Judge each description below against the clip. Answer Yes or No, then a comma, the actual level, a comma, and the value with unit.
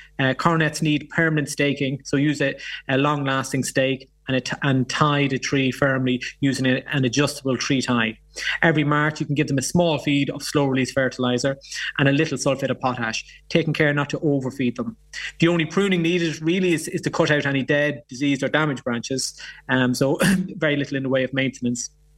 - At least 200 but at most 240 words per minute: Yes, fast, 205 wpm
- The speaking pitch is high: No, medium, 140 Hz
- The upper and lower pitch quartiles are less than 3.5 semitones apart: Yes, average, 2.7 semitones